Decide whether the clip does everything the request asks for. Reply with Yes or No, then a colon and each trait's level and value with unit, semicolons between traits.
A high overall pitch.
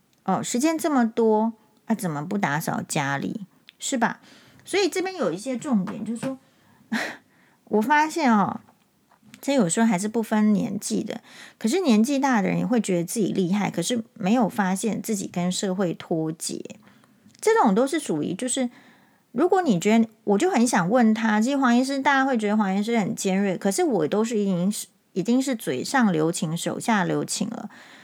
Yes: high, 220 Hz